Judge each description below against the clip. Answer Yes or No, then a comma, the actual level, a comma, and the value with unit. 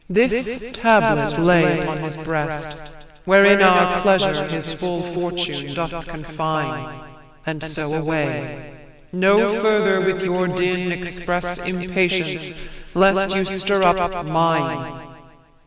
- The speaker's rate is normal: No, slow, 110 wpm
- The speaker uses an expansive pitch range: No, average, 3.2 semitones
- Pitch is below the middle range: No, medium, 175 Hz